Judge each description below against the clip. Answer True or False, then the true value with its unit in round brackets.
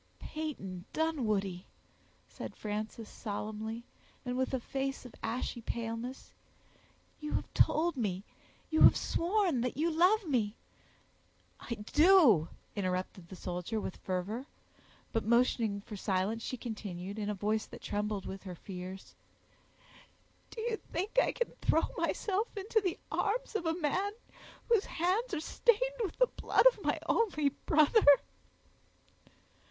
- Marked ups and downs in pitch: True (8.6 semitones)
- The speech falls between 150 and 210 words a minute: False (135 wpm)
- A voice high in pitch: True (245 Hz)